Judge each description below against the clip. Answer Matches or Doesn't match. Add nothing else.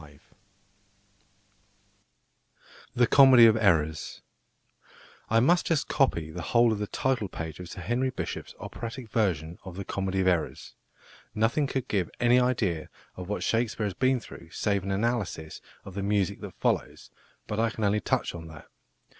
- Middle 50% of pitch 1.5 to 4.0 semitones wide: Doesn't match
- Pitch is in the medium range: Doesn't match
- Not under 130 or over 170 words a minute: Matches